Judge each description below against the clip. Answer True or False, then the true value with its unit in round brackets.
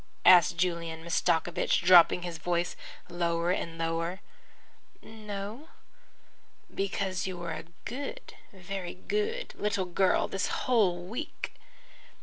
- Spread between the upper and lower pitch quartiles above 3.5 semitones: False (2.7 semitones)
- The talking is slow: True (110 wpm)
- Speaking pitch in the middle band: True (180 Hz)